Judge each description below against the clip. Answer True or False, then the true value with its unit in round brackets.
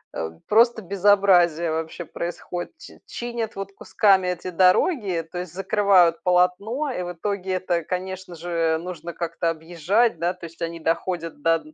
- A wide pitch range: False (2.8 semitones)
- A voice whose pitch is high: False (180 Hz)